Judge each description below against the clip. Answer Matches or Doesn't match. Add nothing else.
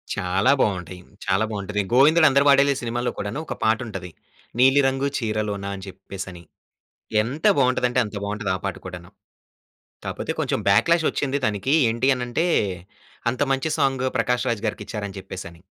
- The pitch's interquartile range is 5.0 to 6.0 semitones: Matches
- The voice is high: Doesn't match